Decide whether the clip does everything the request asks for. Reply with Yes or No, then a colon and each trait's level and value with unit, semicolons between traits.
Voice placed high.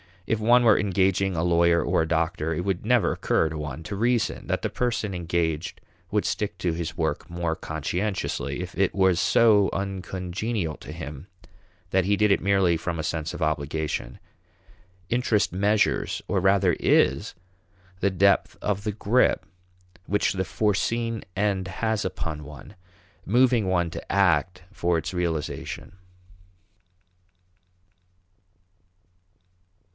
No: very low, 95 Hz